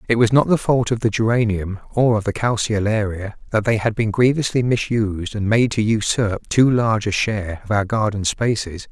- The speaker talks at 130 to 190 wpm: No, average, 200 wpm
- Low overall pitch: Yes, low, 110 Hz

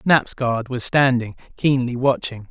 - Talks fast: No, average, 145 wpm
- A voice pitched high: No, low, 125 Hz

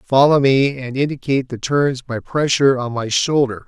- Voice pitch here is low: Yes, low, 130 Hz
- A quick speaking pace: No, average, 180 wpm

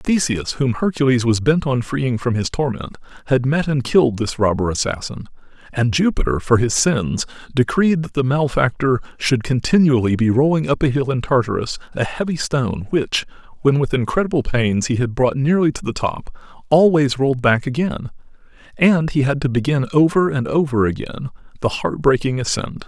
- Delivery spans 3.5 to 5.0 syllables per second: No, 5.3 syllables/s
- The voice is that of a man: Yes, male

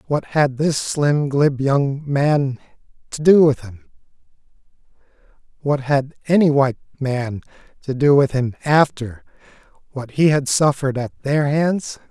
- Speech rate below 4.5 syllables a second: Yes, 4.1 syllables/s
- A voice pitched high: No, medium, 140 Hz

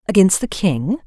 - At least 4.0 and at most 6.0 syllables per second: Yes, 4.8 syllables/s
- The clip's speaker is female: Yes, female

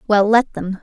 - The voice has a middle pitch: No, high, 205 Hz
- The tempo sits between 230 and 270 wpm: No, fast, 220 wpm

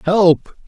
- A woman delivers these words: No, male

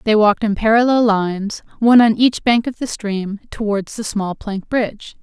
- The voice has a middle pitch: No, high, 215 Hz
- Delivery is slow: No, average, 195 wpm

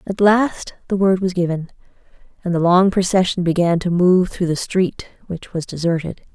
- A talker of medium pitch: Yes, medium, 180 Hz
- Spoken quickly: No, average, 180 wpm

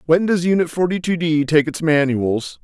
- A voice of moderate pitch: Yes, medium, 160 Hz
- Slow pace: No, fast, 205 wpm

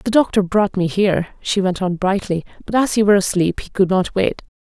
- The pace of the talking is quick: Yes, fast, 235 wpm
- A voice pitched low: No, high, 195 Hz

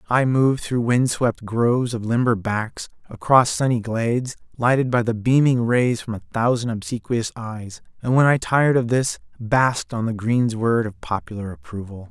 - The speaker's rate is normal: Yes, average, 175 wpm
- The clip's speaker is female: No, male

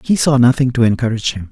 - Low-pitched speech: Yes, low, 120 Hz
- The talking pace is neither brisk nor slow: No, fast, 235 wpm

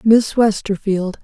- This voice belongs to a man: No, female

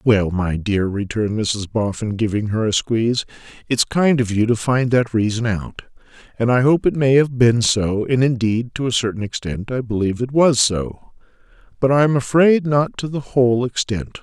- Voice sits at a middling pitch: No, low, 120 Hz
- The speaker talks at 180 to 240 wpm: Yes, average, 200 wpm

